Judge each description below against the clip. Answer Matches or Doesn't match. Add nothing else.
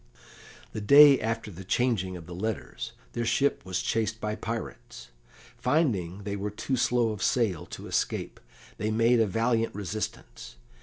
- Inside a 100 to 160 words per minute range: Matches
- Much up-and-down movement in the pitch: Doesn't match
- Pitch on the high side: Doesn't match